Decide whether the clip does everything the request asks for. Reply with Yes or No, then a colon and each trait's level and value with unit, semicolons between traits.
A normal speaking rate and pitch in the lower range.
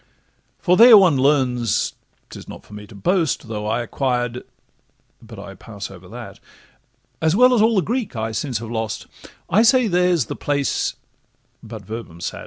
Yes: average, 165 wpm; low, 130 Hz